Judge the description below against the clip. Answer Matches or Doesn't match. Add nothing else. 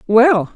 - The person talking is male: Doesn't match